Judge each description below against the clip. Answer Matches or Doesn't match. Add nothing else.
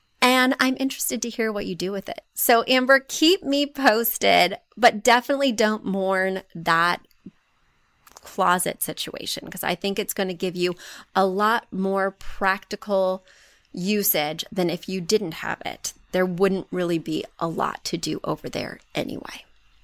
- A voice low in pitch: Doesn't match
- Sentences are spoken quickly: Doesn't match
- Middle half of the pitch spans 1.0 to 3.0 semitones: Doesn't match